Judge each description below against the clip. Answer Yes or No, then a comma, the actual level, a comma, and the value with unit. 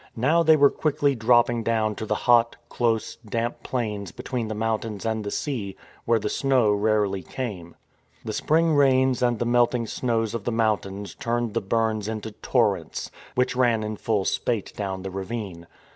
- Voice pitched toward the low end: Yes, low, 115 Hz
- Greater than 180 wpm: No, average, 175 wpm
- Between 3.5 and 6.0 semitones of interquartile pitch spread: No, narrow, 2.6 semitones